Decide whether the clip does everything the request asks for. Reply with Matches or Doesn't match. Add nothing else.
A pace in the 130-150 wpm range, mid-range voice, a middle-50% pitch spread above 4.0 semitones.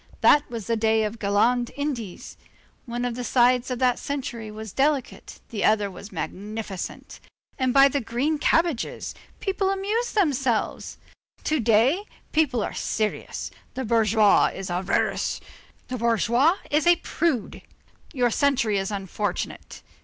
Doesn't match